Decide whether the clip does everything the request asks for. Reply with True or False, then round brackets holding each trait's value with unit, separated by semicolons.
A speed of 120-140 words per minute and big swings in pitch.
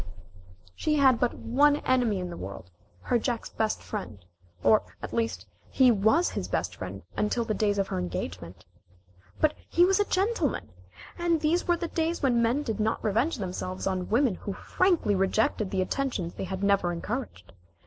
False (180 wpm; 7.2 semitones)